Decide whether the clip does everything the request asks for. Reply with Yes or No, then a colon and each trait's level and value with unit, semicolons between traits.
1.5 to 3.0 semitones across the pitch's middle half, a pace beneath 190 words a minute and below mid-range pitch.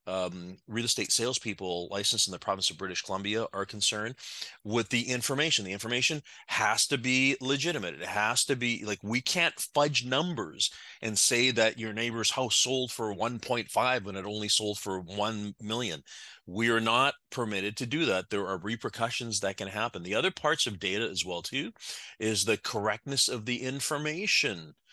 No: average, 4.0 semitones; average, 180 wpm; low, 115 Hz